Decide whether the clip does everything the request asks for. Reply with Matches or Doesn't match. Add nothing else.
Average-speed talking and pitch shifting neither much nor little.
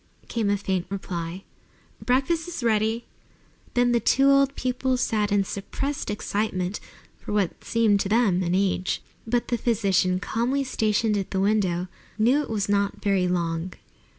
Matches